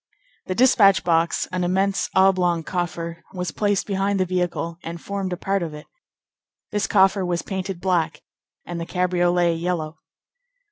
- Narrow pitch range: Yes, narrow, 2.2 semitones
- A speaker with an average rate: Yes, average, 150 wpm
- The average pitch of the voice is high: No, medium, 180 Hz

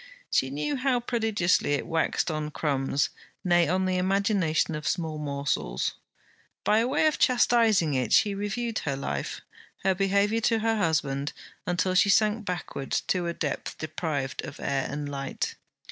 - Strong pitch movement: Yes, wide, 6.5 semitones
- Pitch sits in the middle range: Yes, medium, 175 Hz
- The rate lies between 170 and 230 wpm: No, average, 155 wpm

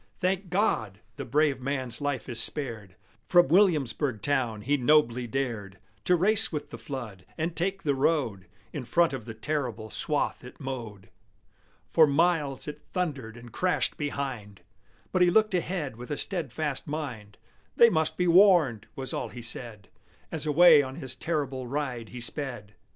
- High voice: No, medium, 140 Hz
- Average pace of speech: Yes, average, 160 wpm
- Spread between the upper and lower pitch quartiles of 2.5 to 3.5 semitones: No, wide, 5.4 semitones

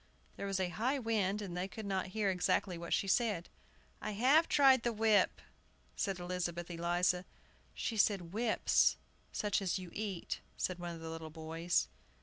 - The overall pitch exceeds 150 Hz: Yes, high, 190 Hz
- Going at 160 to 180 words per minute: Yes, average, 170 wpm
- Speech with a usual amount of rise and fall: Yes, average, 3.6 semitones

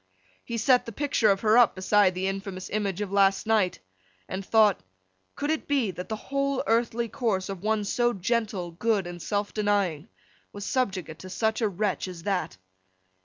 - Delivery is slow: No, average, 180 wpm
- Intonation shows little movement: No, average, 3.4 semitones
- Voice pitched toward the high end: Yes, high, 205 Hz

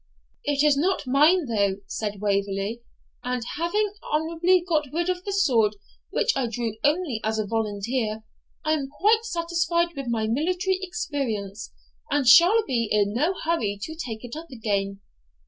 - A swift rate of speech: No, average, 160 wpm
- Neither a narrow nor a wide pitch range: No, wide, 7.6 semitones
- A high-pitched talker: Yes, very high, 275 Hz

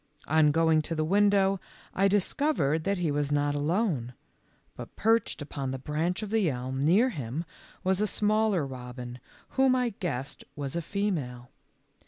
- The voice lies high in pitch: No, medium, 160 Hz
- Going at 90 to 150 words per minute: No, average, 160 wpm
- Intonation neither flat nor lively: No, wide, 6.2 semitones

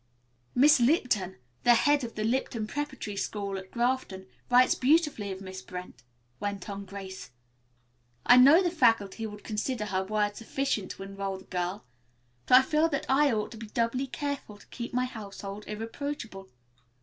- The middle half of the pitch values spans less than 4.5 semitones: No, average, 4.8 semitones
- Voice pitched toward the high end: Yes, high, 220 Hz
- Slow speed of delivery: No, average, 165 wpm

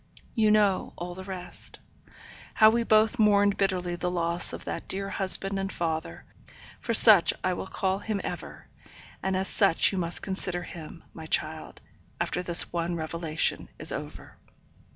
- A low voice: No, medium, 185 Hz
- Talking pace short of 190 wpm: Yes, average, 160 wpm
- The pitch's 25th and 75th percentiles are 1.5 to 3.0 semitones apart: Yes, narrow, 2.6 semitones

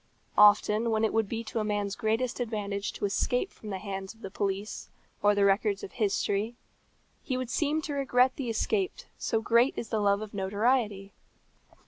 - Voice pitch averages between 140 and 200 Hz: No, high, 215 Hz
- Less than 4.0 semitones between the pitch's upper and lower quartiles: Yes, average, 3.0 semitones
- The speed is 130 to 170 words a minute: No, average, 185 wpm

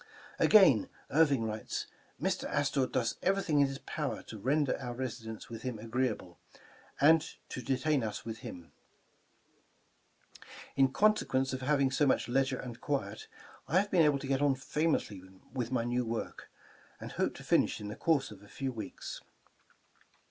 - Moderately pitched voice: No, low, 130 Hz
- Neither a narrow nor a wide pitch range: Yes, average, 3.8 semitones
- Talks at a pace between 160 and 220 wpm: Yes, average, 165 wpm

